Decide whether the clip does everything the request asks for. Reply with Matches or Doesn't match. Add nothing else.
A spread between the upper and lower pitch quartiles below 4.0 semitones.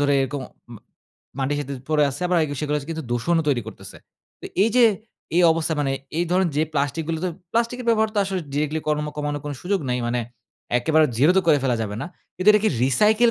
Doesn't match